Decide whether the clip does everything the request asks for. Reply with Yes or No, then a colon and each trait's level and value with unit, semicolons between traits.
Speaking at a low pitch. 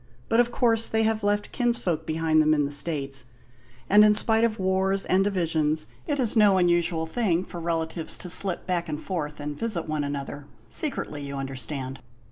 No: medium, 170 Hz